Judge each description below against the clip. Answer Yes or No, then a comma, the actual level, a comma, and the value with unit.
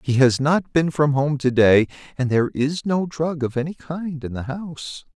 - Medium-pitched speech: Yes, medium, 145 Hz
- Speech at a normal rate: No, fast, 220 wpm